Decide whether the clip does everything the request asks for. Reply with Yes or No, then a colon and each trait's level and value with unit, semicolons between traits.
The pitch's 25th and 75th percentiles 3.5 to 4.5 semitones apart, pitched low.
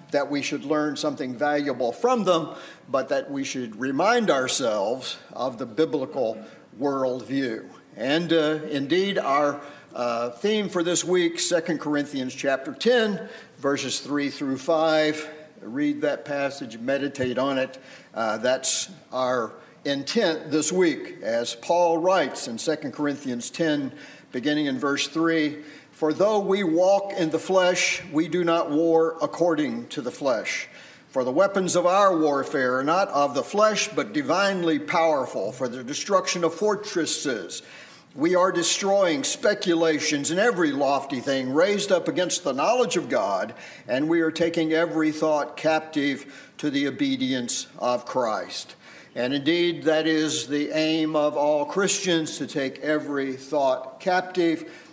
No: average, 4.1 semitones; medium, 155 Hz